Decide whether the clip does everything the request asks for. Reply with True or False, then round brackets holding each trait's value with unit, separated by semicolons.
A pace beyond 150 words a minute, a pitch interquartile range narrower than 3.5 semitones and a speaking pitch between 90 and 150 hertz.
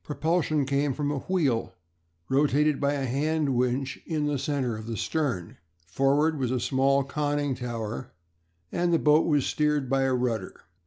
True (165 wpm; 2.8 semitones; 140 Hz)